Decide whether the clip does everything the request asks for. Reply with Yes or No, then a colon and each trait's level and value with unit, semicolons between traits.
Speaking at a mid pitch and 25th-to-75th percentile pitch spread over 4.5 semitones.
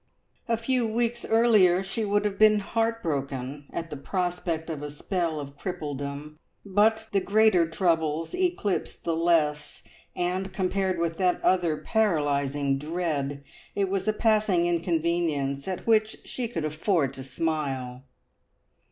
Yes: medium, 175 Hz; wide, 5.6 semitones